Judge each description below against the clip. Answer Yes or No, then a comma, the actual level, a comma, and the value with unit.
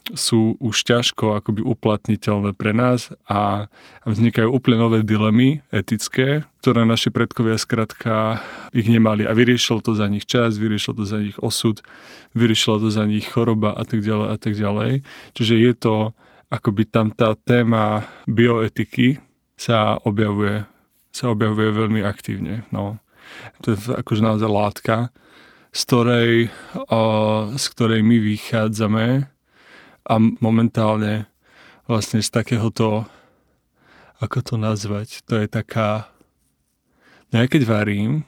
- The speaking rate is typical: Yes, average, 130 wpm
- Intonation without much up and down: Yes, narrow, 1.6 semitones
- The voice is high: No, low, 110 Hz